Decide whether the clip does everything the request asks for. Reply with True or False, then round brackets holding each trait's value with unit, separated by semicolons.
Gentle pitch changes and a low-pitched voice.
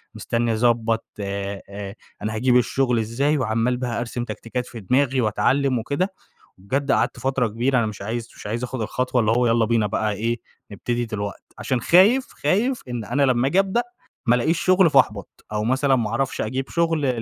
False (3.5 semitones; 120 Hz)